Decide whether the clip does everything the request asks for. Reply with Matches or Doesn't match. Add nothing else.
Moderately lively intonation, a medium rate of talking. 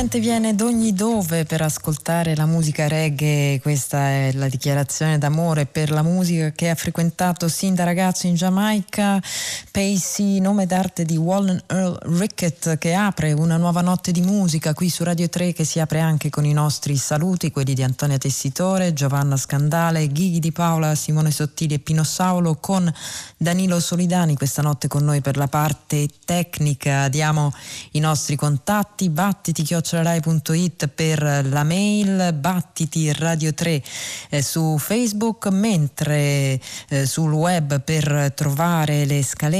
Matches